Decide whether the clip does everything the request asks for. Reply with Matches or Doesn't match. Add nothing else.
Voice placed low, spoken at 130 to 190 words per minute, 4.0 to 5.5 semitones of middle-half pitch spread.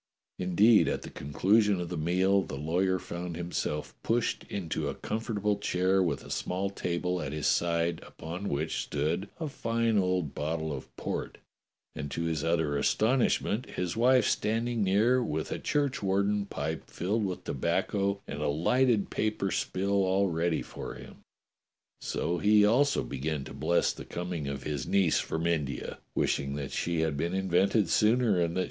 Matches